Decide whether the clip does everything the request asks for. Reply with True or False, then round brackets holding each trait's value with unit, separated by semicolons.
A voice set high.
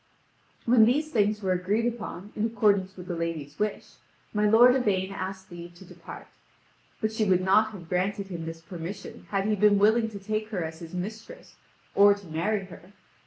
True (200 Hz)